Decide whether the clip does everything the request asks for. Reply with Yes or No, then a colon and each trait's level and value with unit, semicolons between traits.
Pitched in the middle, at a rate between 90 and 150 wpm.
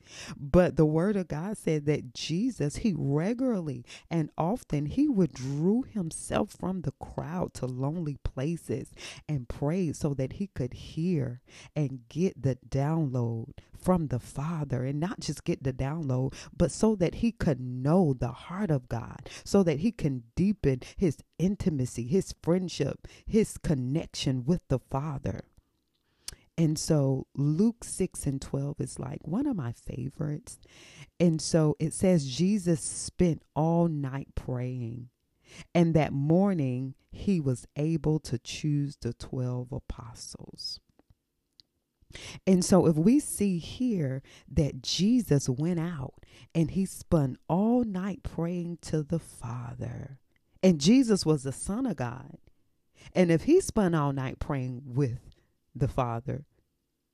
Yes: medium, 150 Hz; average, 140 wpm